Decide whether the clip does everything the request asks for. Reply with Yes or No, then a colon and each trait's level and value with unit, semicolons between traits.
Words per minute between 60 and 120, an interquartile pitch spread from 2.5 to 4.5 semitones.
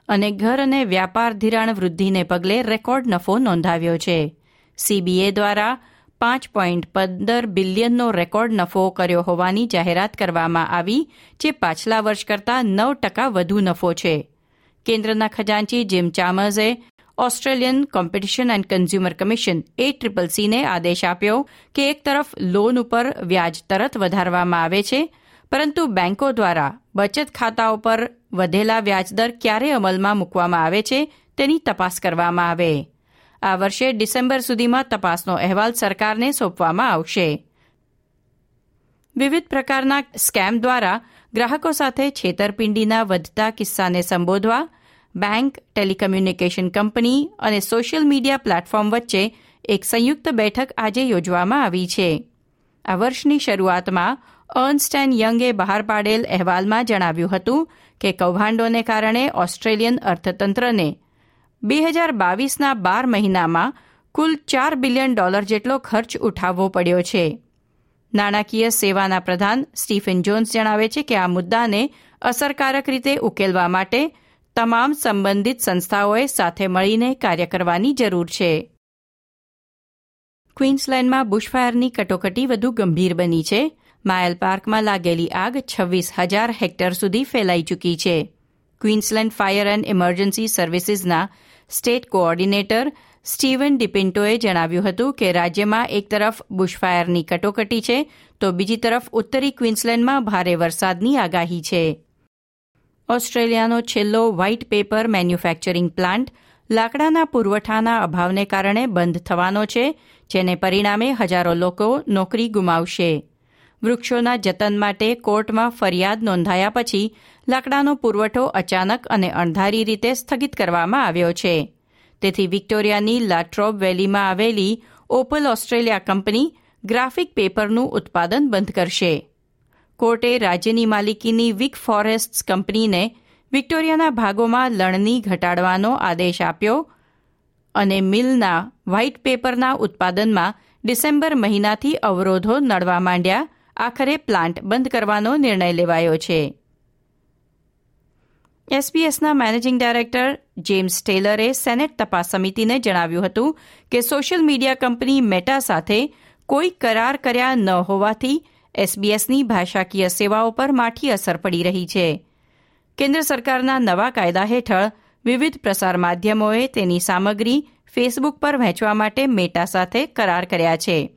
No: average, 115 wpm; average, 4.9 semitones